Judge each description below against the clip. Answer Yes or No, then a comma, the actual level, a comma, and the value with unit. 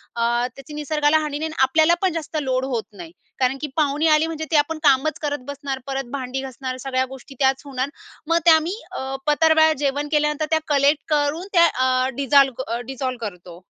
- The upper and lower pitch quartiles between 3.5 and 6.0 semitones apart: No, average, 3.0 semitones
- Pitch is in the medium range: No, very high, 280 Hz